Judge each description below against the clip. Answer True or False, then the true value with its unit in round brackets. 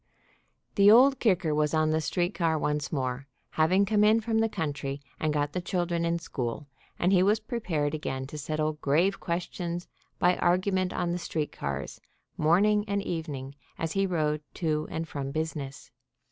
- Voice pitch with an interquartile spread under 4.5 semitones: True (3.8 semitones)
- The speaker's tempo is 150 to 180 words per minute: True (175 wpm)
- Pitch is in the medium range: True (165 Hz)